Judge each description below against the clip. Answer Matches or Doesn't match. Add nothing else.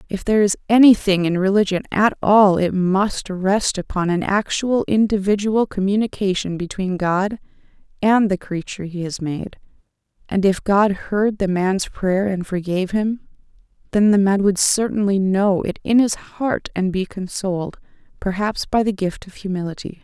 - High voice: Matches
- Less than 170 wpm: Matches